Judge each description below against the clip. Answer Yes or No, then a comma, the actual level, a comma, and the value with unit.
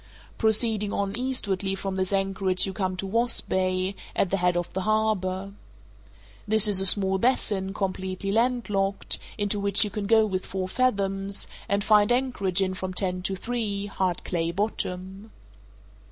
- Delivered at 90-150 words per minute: No, average, 160 wpm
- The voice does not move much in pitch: Yes, narrow, 2.1 semitones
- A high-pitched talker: Yes, high, 195 Hz